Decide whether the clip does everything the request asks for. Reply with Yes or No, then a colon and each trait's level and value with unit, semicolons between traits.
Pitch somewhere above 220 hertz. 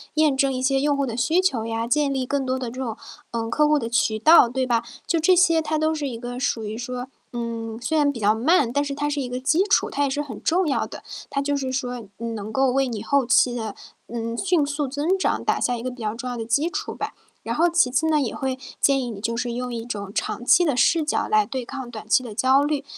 Yes: very high, 260 Hz